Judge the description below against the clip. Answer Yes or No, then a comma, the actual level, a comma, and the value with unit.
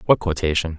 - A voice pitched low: Yes, very low, 85 Hz